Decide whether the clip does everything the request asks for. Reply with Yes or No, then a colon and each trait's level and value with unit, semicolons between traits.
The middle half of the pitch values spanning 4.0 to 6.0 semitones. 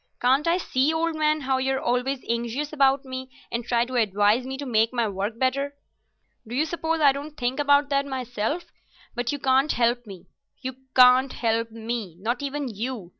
No: average, 3.2 semitones